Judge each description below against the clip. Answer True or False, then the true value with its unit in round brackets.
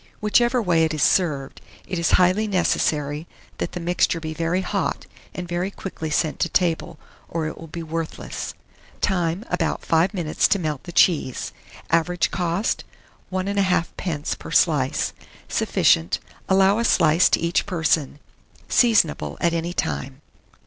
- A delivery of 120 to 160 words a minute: True (150 wpm)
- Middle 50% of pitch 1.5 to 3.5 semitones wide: True (2.7 semitones)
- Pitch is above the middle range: False (170 Hz)